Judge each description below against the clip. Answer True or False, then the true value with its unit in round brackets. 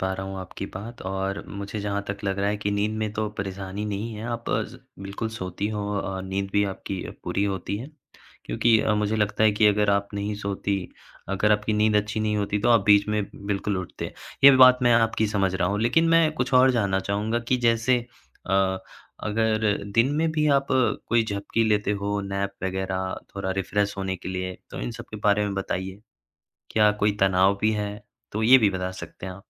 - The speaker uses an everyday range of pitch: False (2.0 semitones)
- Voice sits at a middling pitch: False (105 Hz)